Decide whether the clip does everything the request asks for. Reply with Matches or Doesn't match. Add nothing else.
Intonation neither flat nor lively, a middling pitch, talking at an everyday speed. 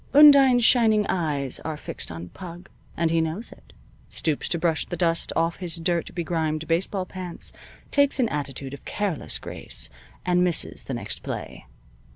Matches